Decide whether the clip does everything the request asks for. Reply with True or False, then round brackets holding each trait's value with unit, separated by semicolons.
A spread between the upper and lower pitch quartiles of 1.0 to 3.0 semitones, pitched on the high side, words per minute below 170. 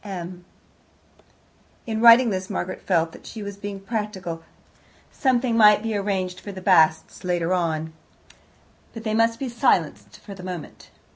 False (3.9 semitones; 195 Hz; 150 wpm)